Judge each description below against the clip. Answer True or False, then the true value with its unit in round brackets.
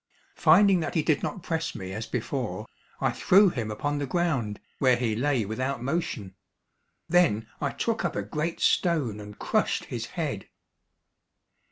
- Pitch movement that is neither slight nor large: False (7.3 semitones)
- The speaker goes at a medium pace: True (160 wpm)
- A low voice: False (145 Hz)